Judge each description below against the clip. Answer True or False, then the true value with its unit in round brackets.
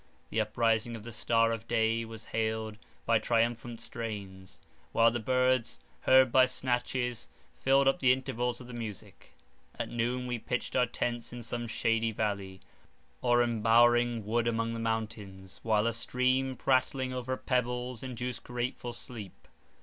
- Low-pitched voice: True (120 Hz)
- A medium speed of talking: True (150 wpm)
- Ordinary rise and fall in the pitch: False (1.8 semitones)